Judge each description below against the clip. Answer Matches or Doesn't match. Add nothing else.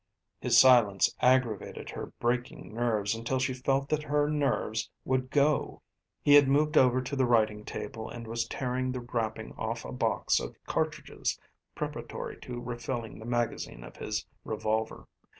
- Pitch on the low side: Matches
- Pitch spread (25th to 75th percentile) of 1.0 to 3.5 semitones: Matches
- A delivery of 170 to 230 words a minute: Doesn't match